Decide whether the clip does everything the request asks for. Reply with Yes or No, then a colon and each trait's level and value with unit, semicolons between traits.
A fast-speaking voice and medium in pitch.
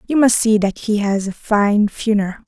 No: fast, 220 wpm; high, 215 Hz